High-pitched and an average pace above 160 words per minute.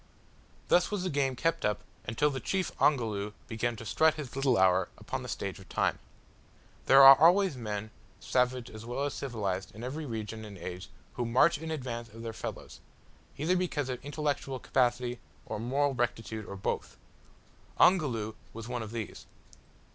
No: low, 125 Hz; average, 170 wpm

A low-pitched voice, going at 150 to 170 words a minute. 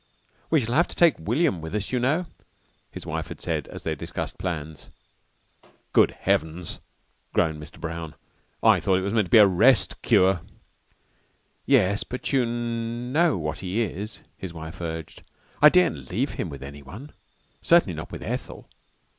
Yes: very low, 95 Hz; average, 165 wpm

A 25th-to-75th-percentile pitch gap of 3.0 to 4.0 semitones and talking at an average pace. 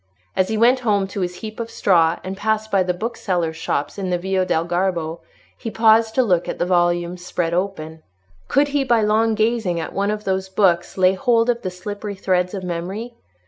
No: average, 3.7 semitones; fast, 210 wpm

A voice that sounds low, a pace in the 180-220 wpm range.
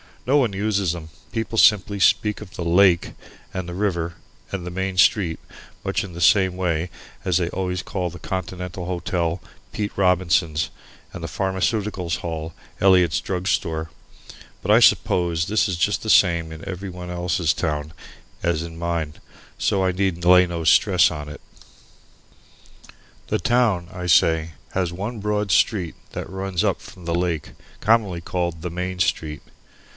No: very low, 90 Hz; average, 160 wpm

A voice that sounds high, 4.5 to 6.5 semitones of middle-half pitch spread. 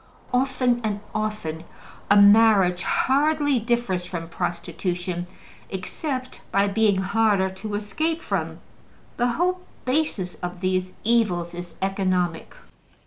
Yes: high, 205 Hz; average, 5.1 semitones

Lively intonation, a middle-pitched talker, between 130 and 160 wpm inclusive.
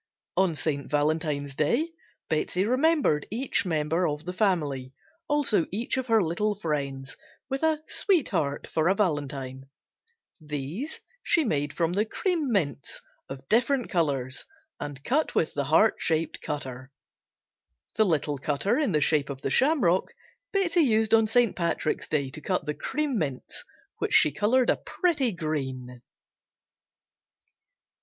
Yes: wide, 8.3 semitones; medium, 165 Hz; average, 140 wpm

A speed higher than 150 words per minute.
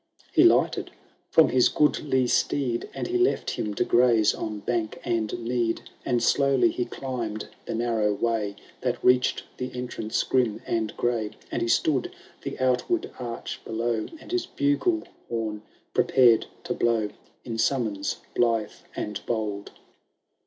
No: average, 145 wpm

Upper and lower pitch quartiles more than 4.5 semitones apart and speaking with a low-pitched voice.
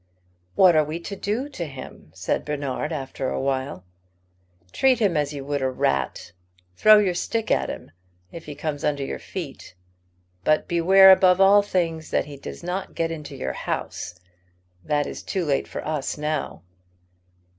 No: average, 4.9 semitones; medium, 155 Hz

